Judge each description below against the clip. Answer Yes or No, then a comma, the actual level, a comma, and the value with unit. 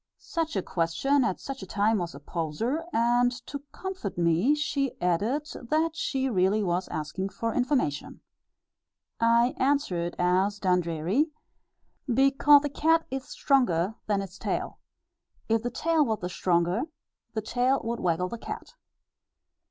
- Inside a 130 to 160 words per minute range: Yes, average, 145 wpm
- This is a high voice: Yes, high, 225 Hz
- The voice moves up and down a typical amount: No, wide, 7.2 semitones